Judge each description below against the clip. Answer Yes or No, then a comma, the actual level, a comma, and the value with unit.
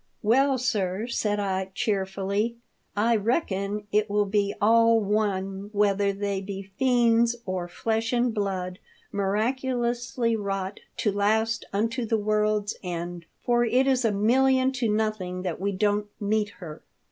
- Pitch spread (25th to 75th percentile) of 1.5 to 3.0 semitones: Yes, average, 2.7 semitones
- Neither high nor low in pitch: No, high, 210 Hz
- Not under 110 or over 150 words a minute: Yes, average, 145 wpm